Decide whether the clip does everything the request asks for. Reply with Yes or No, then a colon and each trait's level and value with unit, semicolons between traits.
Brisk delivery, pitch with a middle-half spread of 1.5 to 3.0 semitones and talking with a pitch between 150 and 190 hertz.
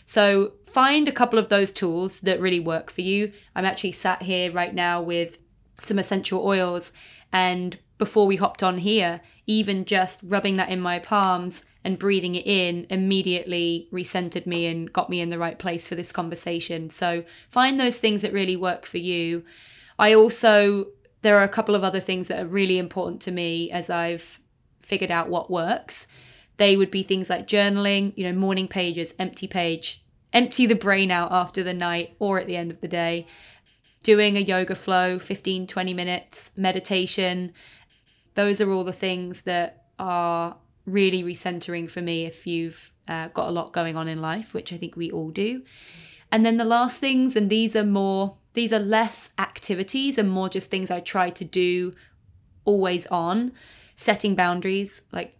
No: average, 185 wpm; narrow, 2.5 semitones; medium, 185 Hz